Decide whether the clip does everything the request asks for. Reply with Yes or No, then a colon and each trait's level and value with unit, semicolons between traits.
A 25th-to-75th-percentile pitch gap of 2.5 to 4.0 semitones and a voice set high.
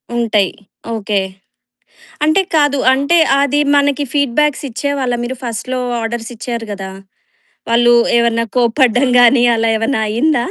Yes: average, 3.6 semitones; high, 245 Hz